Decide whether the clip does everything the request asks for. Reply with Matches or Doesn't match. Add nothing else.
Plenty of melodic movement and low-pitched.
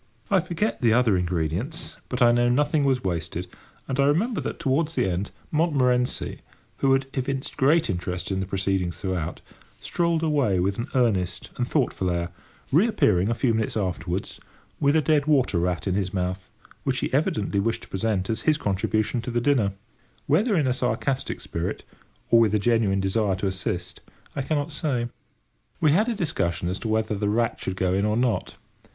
Matches